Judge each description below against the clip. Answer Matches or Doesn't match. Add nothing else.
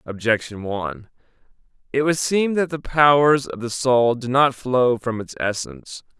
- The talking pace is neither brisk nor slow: Matches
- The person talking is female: Doesn't match